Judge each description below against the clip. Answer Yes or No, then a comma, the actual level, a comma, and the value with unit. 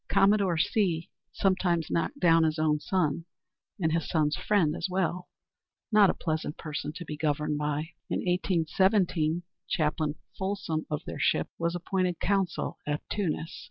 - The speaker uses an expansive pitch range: No, average, 3.3 semitones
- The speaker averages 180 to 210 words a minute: No, average, 150 wpm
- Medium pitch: Yes, medium, 170 Hz